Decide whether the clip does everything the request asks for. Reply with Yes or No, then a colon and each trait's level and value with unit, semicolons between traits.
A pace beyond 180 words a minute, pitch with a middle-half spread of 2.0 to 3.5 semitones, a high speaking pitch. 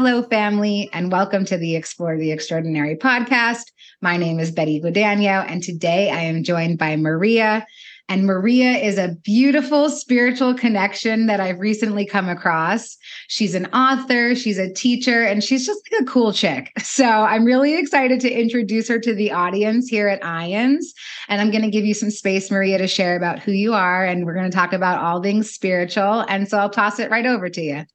No: average, 200 wpm; average, 4.4 semitones; high, 205 Hz